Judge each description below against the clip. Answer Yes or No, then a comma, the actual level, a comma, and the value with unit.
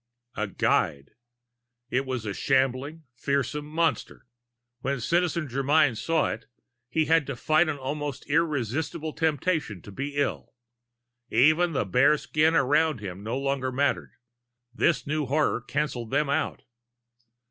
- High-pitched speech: No, medium, 140 Hz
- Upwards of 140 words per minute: No, slow, 135 wpm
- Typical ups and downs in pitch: Yes, average, 3.6 semitones